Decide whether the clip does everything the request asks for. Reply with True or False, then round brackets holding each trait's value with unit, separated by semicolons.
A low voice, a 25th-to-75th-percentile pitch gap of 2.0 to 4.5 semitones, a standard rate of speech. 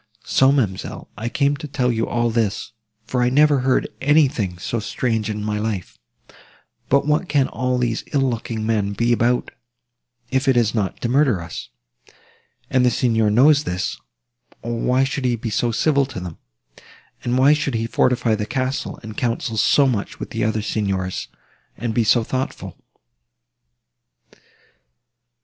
True (120 Hz; 3.4 semitones; 165 wpm)